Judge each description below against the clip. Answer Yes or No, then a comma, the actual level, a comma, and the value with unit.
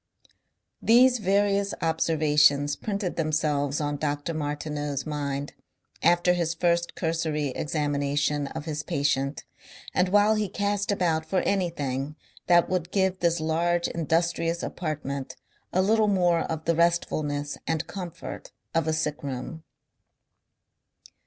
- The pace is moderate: No, slow, 120 wpm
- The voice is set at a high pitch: No, medium, 160 Hz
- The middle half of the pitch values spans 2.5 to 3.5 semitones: Yes, average, 3.2 semitones